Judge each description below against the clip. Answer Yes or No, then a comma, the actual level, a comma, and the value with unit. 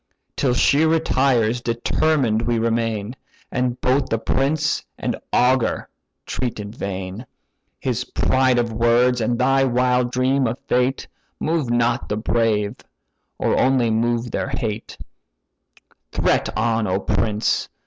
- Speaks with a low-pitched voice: Yes, low, 120 Hz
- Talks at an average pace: No, slow, 130 wpm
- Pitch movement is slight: Yes, narrow, 2.3 semitones